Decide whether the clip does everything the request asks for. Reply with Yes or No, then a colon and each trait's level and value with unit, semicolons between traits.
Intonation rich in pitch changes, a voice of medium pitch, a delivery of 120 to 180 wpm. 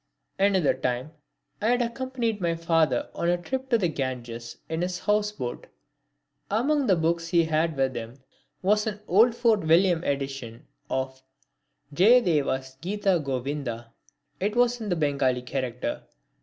Yes: wide, 7.8 semitones; medium, 165 Hz; average, 140 wpm